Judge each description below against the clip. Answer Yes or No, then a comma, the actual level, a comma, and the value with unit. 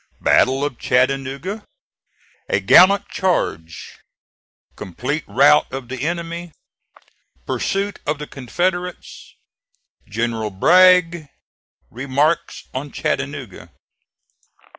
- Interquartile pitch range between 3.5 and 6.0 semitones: Yes, average, 5.3 semitones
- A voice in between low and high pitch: Yes, medium, 145 Hz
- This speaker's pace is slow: Yes, slow, 80 wpm